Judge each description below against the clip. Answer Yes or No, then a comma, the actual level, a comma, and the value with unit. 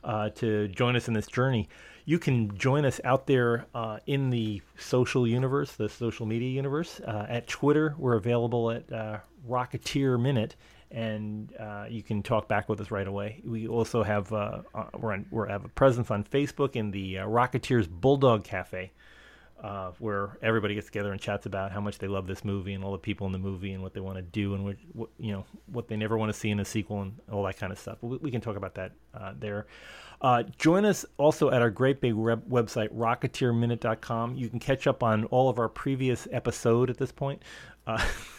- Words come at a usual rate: No, fast, 215 wpm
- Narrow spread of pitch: No, average, 3.4 semitones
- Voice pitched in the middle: No, low, 115 Hz